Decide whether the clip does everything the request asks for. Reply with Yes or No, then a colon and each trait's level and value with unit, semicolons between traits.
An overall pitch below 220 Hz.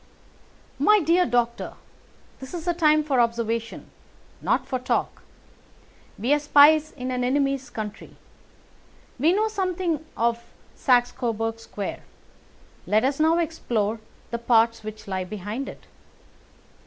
No: very high, 250 Hz